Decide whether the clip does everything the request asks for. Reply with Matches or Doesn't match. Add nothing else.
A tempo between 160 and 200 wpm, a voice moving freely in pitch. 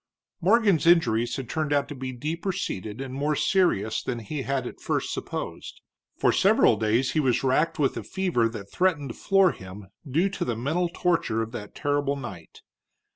Matches